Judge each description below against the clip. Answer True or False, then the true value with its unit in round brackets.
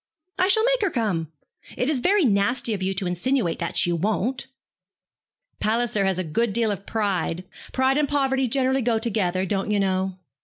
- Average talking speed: True (185 wpm)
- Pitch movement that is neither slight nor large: False (5.7 semitones)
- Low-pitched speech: False (220 Hz)